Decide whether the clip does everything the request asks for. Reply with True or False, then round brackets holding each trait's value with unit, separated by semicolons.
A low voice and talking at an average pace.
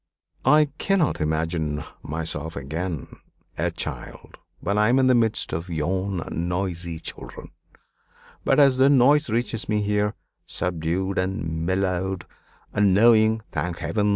False (95 Hz; 130 wpm)